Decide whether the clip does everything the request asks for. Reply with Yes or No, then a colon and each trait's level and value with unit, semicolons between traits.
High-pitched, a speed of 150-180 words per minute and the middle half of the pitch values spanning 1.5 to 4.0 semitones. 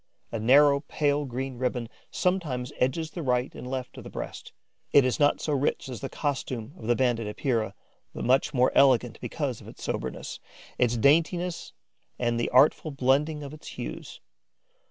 No: low, 130 Hz; average, 175 wpm; average, 2.9 semitones